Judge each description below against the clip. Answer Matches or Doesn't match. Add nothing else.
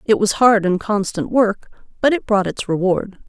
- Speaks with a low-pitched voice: Doesn't match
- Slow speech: Doesn't match